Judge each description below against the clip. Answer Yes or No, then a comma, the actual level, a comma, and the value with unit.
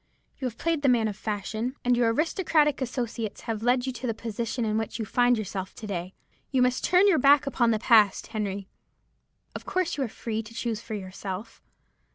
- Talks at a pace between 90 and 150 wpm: No, fast, 205 wpm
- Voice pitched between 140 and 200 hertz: No, high, 230 Hz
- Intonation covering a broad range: No, average, 3.2 semitones